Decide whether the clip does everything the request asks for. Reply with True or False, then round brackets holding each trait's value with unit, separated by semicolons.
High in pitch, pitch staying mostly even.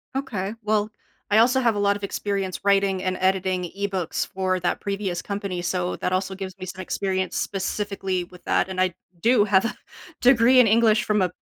True (195 Hz; 2.1 semitones)